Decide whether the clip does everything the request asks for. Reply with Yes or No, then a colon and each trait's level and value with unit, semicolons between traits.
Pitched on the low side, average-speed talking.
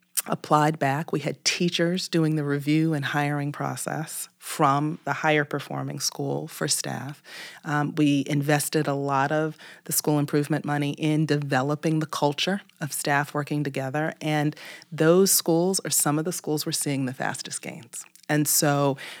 No: medium, 150 Hz; average, 160 wpm